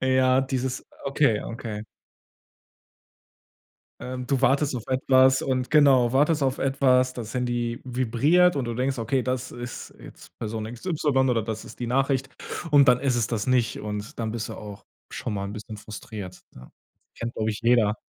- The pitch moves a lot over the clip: No, average, 2.9 semitones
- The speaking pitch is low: Yes, low, 125 Hz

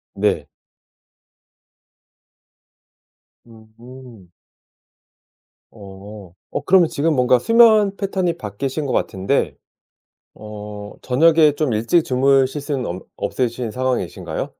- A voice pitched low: Yes, low, 125 Hz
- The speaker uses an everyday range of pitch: No, wide, 6.3 semitones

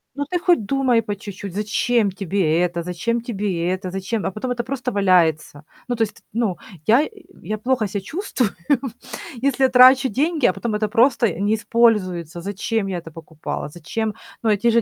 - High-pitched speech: Yes, high, 215 Hz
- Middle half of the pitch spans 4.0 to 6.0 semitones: Yes, average, 4.6 semitones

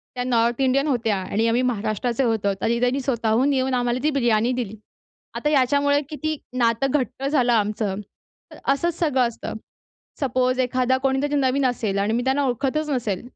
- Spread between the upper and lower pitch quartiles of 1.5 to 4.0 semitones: Yes, average, 2.9 semitones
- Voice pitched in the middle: No, very high, 250 Hz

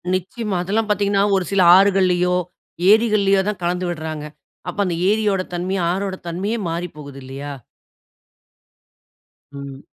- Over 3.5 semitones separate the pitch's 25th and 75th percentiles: No, average, 3.0 semitones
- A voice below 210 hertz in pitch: Yes, medium, 185 Hz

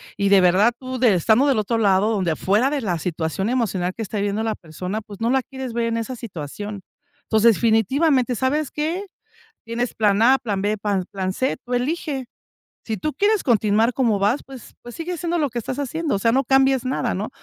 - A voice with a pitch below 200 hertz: No, high, 230 Hz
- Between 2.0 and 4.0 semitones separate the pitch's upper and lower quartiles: No, average, 4.5 semitones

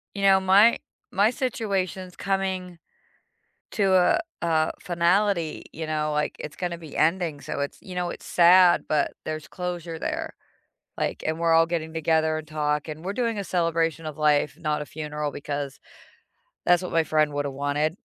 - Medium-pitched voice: Yes, medium, 165 Hz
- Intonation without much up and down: No, average, 3.2 semitones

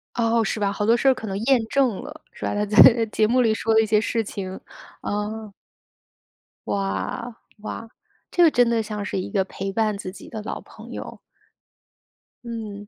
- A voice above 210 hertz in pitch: Yes, high, 220 Hz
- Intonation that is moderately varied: No, narrow, 2.0 semitones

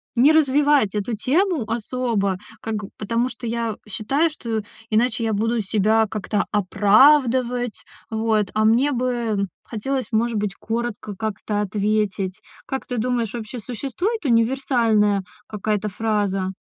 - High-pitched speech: Yes, high, 225 Hz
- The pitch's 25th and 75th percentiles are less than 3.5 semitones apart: Yes, average, 3.0 semitones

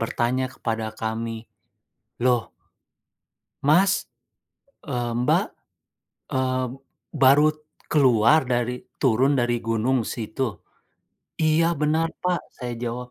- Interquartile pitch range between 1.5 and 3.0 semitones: No, average, 3.8 semitones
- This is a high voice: No, low, 125 Hz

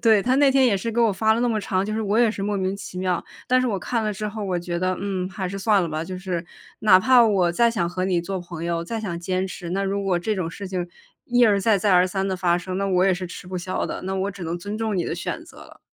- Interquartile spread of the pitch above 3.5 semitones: No, average, 3.0 semitones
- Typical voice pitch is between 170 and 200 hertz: Yes, high, 190 Hz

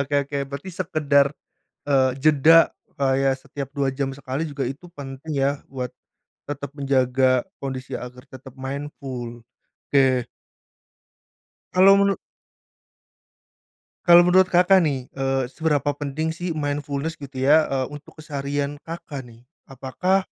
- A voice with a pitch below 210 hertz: Yes, medium, 140 Hz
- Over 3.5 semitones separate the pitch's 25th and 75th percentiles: No, average, 2.7 semitones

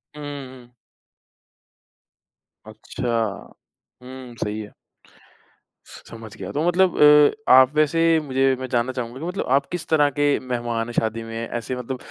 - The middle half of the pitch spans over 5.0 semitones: No, average, 3.5 semitones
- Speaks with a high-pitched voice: No, low, 130 Hz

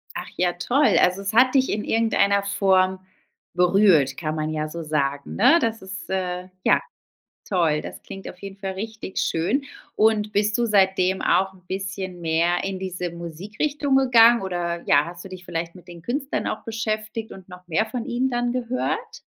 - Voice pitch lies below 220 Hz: Yes, high, 190 Hz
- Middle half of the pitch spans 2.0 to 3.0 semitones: No, average, 4.0 semitones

